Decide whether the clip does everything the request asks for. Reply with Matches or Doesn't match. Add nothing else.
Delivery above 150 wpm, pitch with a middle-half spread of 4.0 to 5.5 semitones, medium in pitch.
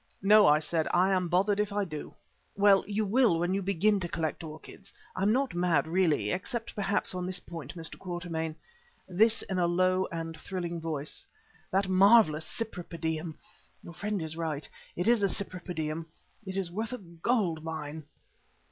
Doesn't match